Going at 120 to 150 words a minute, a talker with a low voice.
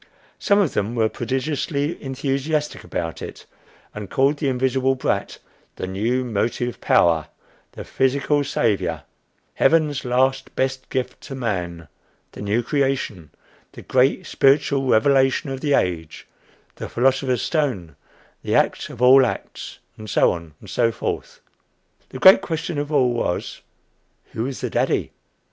Yes: average, 140 wpm; low, 130 Hz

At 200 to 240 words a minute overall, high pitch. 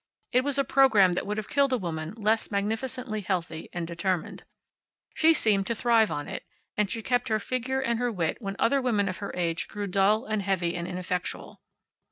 Yes: fast, 205 wpm; high, 210 Hz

